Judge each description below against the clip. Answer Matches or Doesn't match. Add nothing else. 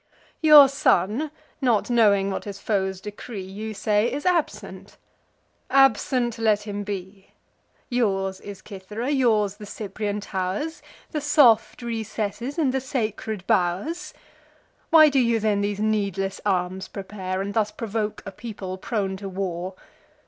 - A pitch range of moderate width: Matches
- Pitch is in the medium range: Doesn't match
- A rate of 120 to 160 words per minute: Matches